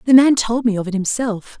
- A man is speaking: No, female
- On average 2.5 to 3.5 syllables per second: No, 5.5 syllables/s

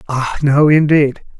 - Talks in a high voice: No, medium, 145 Hz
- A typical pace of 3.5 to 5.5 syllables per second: Yes, 3.9 syllables/s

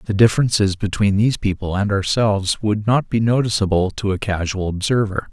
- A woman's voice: No, male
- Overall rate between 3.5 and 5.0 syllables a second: No, 5.6 syllables/s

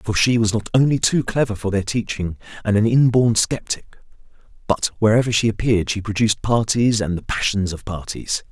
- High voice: No, low, 110 Hz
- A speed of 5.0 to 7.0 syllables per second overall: Yes, 5.5 syllables/s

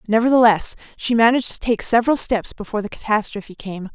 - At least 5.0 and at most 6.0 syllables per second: No, 6.4 syllables/s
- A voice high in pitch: Yes, high, 220 Hz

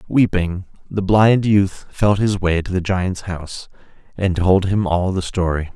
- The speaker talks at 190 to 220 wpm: No, average, 175 wpm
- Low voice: Yes, very low, 95 Hz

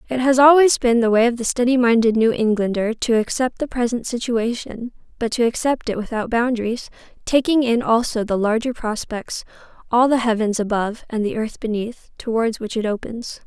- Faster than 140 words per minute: Yes, average, 170 wpm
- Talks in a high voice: Yes, high, 235 Hz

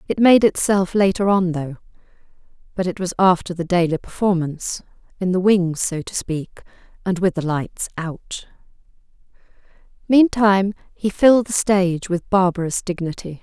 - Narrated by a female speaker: Yes, female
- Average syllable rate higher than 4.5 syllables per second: Yes, 4.9 syllables/s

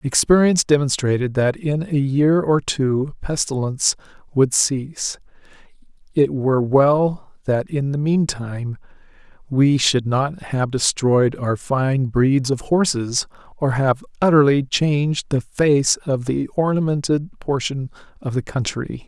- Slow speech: Yes, slow, 130 wpm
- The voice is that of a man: Yes, male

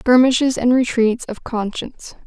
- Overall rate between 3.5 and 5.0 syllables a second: Yes, 4.7 syllables/s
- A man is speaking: No, female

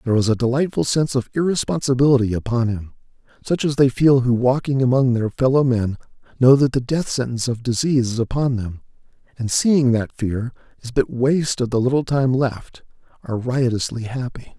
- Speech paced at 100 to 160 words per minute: No, average, 180 wpm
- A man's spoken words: Yes, male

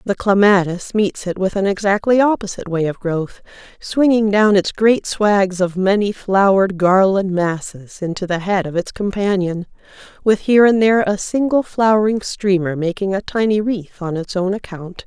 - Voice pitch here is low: No, high, 195 Hz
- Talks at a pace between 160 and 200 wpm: Yes, average, 170 wpm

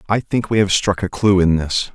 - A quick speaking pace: Yes, fast, 275 wpm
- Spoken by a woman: No, male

